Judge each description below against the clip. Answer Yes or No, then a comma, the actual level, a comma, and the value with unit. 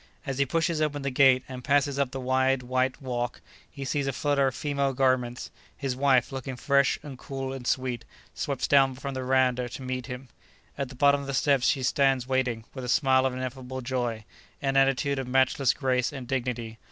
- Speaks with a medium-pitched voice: No, low, 130 Hz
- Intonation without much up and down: Yes, narrow, 1.5 semitones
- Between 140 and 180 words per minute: No, fast, 205 wpm